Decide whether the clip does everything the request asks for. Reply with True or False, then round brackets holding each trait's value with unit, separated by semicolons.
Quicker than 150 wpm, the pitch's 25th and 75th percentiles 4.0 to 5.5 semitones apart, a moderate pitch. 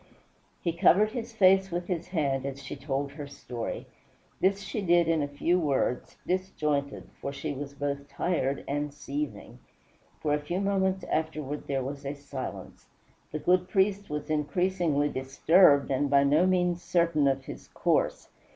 True (160 wpm; 4.4 semitones; 150 Hz)